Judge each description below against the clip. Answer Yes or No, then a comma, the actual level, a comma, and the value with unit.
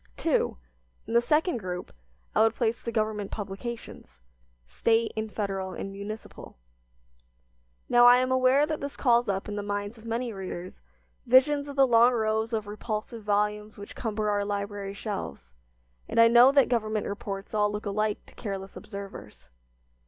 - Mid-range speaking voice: No, high, 215 Hz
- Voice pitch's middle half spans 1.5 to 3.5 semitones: Yes, average, 2.8 semitones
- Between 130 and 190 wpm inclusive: Yes, average, 165 wpm